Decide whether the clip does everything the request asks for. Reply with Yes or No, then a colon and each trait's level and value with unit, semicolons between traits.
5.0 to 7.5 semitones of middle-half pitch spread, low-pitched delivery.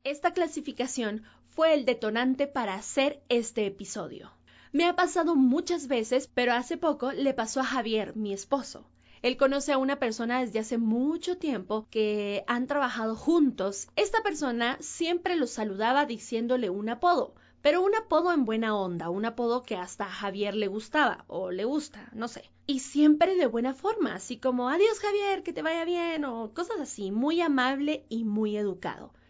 No: wide, 5.6 semitones; very high, 255 Hz